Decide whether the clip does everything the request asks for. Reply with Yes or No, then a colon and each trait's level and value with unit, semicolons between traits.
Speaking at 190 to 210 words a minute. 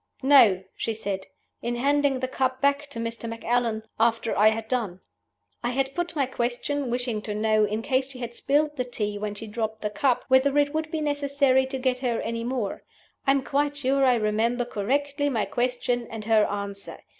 Yes: average, 200 wpm